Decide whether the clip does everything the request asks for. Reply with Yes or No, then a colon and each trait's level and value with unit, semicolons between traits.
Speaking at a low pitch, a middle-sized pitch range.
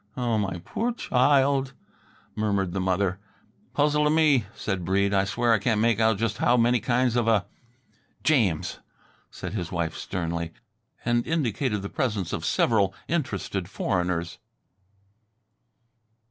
Yes: low, 110 Hz; average, 4.6 semitones